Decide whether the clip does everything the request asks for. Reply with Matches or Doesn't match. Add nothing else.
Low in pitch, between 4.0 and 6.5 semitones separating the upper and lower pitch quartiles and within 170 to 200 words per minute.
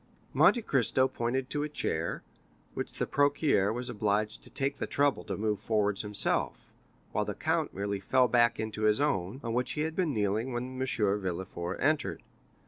Matches